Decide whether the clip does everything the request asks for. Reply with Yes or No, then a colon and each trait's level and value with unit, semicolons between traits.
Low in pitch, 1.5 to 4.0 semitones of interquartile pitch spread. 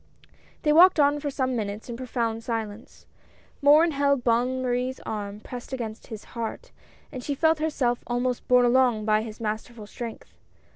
No: high, 245 Hz; average, 3.7 semitones